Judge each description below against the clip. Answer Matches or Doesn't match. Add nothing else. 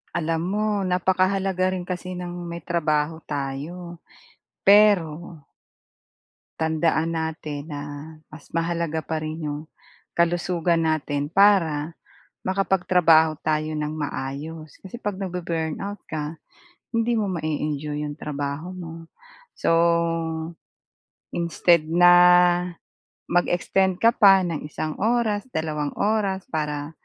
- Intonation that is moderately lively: Matches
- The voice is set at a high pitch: Doesn't match